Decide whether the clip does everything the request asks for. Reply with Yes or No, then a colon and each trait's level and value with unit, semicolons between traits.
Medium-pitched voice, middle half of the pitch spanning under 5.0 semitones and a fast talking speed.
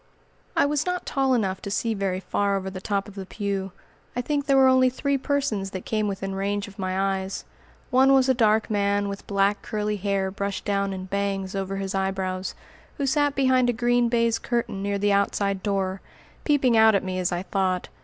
No: high, 200 Hz; average, 3.9 semitones; fast, 210 wpm